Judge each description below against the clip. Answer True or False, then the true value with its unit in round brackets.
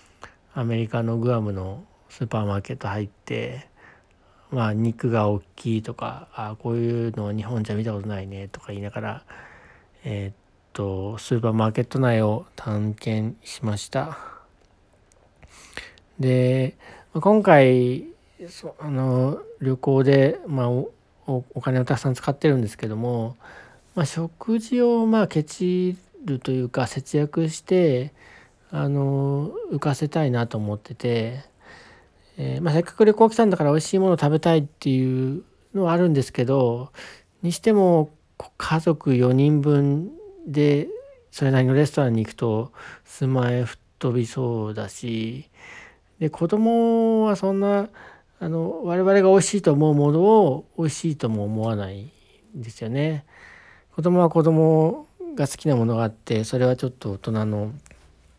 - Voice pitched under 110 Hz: False (130 Hz)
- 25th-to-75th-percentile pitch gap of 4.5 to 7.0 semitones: True (6.4 semitones)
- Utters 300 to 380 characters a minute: False (285 characters per minute)